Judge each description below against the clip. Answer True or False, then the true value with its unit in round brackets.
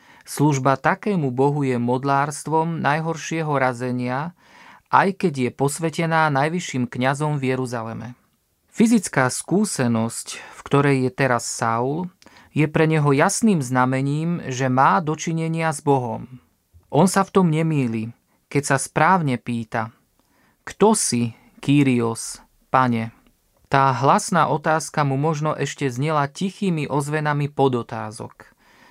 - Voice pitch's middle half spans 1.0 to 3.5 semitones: False (4.0 semitones)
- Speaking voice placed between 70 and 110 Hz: False (140 Hz)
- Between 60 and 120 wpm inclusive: True (115 wpm)